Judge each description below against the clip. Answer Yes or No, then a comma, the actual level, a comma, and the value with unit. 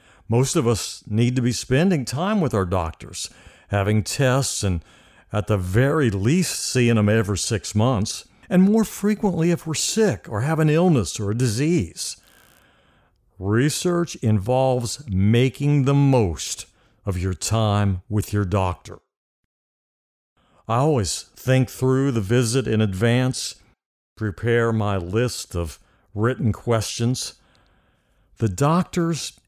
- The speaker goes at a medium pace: No, slow, 130 wpm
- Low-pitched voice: Yes, low, 115 Hz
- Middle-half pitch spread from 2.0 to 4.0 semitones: No, average, 4.8 semitones